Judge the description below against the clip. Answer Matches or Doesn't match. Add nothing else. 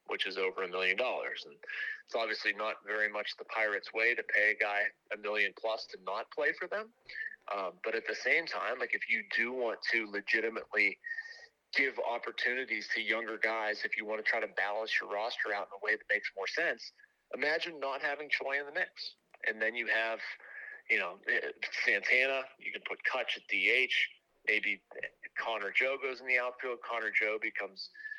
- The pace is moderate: Matches